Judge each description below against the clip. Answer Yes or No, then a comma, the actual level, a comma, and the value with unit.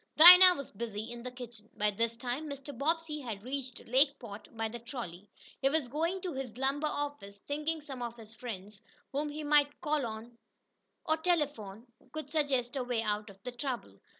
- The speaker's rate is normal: Yes, average, 185 wpm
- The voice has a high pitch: Yes, very high, 255 Hz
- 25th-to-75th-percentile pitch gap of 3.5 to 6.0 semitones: Yes, average, 4.7 semitones